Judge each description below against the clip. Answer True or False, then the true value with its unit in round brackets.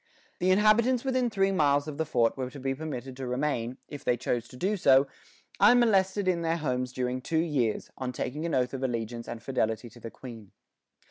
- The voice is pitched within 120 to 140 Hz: True (135 Hz)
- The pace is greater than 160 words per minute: True (205 wpm)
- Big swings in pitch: True (6.4 semitones)